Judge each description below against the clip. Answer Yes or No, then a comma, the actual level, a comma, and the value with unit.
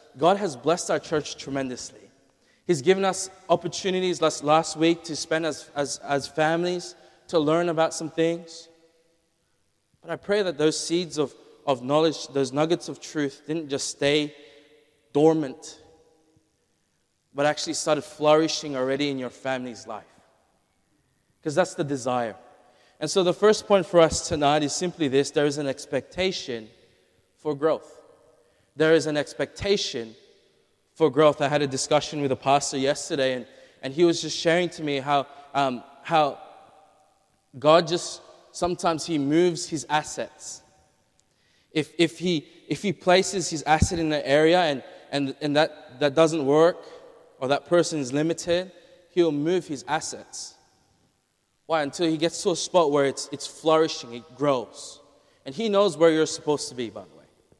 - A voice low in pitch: No, medium, 155 Hz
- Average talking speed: Yes, average, 160 wpm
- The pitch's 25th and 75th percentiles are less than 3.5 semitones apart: Yes, average, 2.8 semitones